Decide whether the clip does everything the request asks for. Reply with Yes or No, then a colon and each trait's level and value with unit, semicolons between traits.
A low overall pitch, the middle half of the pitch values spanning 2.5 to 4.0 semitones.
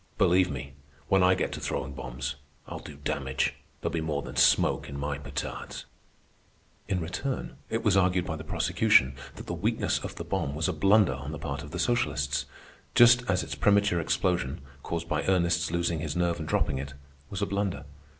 No: very low, 80 Hz; average, 4.5 semitones